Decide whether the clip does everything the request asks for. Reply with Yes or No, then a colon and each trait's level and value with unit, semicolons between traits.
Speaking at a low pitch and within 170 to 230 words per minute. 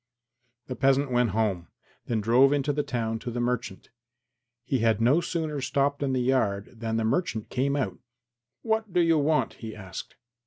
Yes: low, 125 Hz; average, 180 wpm